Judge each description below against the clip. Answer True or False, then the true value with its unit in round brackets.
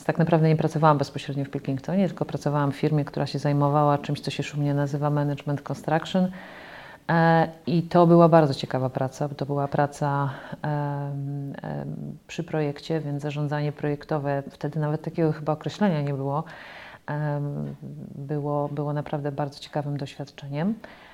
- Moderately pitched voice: True (145 Hz)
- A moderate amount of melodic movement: False (1.6 semitones)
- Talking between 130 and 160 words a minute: True (140 wpm)